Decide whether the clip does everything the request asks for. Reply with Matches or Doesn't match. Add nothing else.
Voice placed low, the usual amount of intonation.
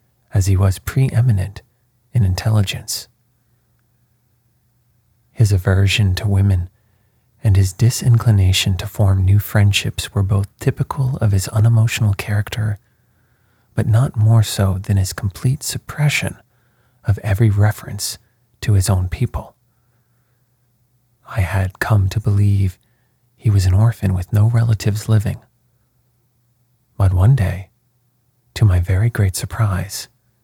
Matches